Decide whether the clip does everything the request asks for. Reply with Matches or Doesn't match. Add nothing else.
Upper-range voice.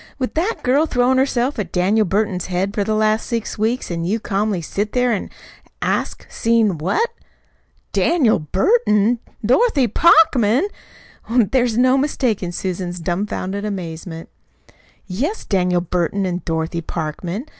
Matches